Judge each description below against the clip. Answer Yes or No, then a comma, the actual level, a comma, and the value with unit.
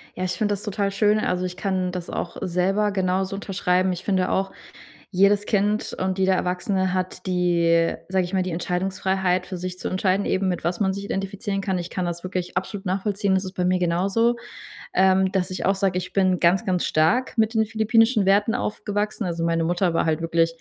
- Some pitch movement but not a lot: No, narrow, 1.8 semitones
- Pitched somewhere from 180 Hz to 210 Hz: Yes, high, 190 Hz